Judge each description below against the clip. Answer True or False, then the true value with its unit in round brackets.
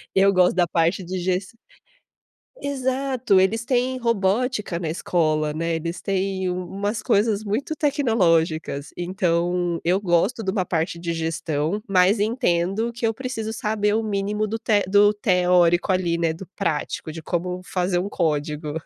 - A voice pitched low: False (190 Hz)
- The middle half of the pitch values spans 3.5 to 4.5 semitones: True (4.0 semitones)